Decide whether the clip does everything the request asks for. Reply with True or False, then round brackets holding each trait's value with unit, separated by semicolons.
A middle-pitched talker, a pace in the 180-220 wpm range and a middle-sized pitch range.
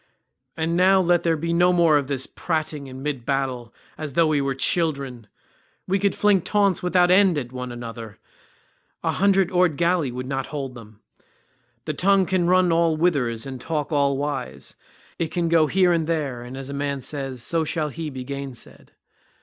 True (150 Hz; 190 wpm; 4.5 semitones)